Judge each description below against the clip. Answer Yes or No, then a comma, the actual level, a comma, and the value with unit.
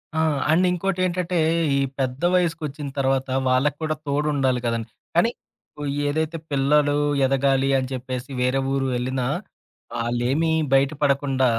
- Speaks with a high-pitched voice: No, low, 135 Hz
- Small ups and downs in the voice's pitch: No, average, 3.1 semitones